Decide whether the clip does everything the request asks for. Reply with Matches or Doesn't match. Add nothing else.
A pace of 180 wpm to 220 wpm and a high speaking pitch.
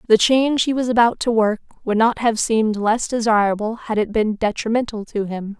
Matches